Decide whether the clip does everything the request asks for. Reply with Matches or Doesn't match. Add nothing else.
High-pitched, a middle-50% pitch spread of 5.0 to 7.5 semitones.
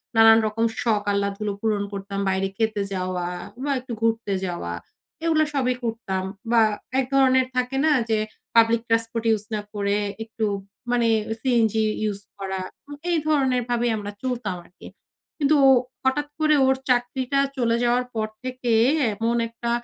Doesn't match